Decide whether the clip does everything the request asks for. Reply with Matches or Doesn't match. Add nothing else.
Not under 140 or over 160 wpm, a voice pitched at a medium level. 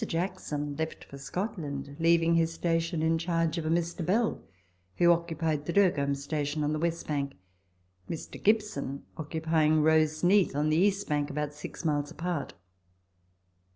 Matches